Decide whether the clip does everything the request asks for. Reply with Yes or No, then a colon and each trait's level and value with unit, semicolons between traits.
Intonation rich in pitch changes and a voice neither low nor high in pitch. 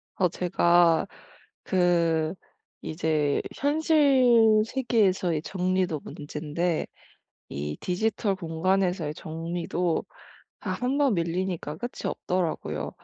No: average, 4.1 semitones; medium, 180 Hz